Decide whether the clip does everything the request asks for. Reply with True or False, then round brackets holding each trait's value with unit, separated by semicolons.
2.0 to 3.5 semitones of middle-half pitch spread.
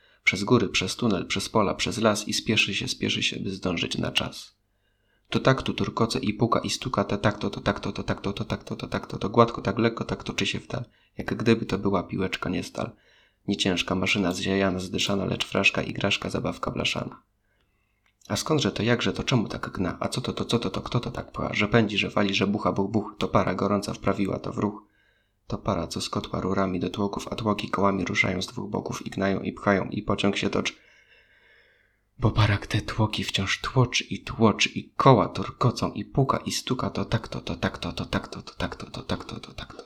True (2.5 semitones)